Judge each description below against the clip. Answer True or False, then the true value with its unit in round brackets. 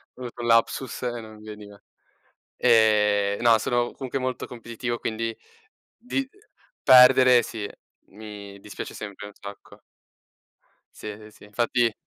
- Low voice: True (115 Hz)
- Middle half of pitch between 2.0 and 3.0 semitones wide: True (2.6 semitones)